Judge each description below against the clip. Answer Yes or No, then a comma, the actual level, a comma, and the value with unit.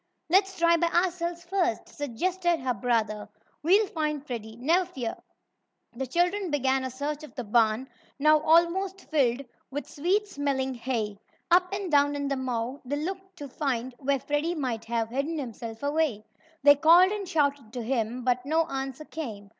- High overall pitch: Yes, very high, 285 Hz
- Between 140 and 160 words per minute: No, average, 170 wpm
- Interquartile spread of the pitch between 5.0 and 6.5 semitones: Yes, wide, 5.4 semitones